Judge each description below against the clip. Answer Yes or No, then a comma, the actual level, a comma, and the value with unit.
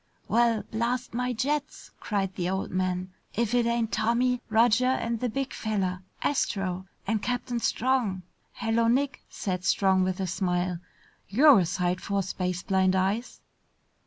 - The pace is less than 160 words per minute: Yes, average, 150 wpm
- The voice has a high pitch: Yes, high, 215 Hz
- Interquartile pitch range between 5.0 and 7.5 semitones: No, average, 4.4 semitones